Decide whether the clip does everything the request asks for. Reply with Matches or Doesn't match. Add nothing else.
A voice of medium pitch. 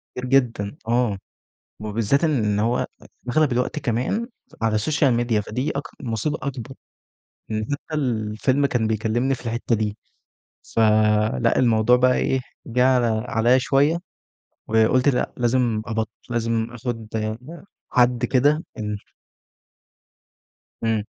Doesn't match